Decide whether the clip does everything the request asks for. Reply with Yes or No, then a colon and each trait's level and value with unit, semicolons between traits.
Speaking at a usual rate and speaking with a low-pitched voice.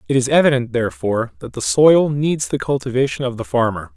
Yes: average, 195 wpm; low, 130 Hz